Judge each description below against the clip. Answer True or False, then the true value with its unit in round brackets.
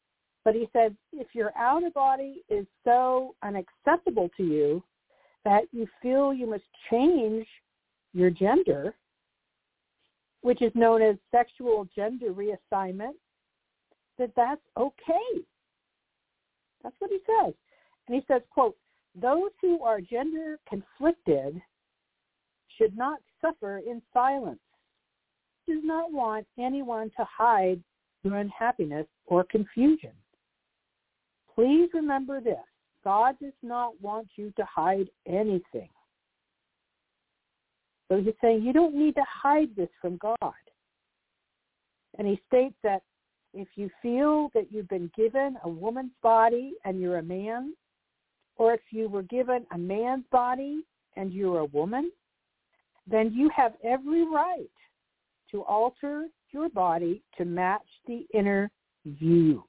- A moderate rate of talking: False (125 wpm)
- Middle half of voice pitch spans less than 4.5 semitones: False (5.4 semitones)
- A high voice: True (235 Hz)